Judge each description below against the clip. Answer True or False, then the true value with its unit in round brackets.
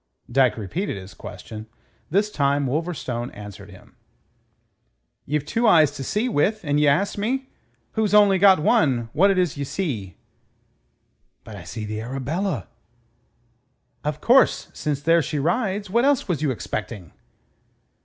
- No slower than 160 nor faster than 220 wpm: False (145 wpm)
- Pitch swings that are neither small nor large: False (8.3 semitones)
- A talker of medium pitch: True (150 Hz)